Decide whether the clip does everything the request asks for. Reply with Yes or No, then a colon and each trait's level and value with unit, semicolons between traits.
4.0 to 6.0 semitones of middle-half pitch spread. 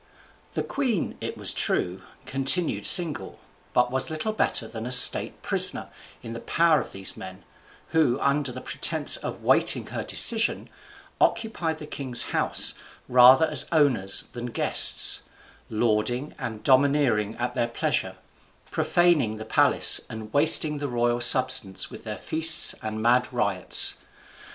Yes: average, 5.1 semitones